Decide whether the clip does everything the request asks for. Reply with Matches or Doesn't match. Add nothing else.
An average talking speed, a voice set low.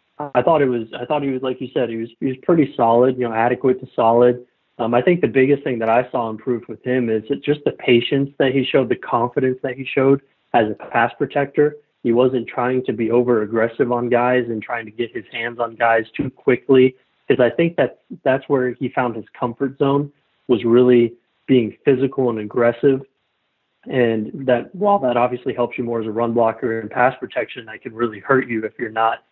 Doesn't match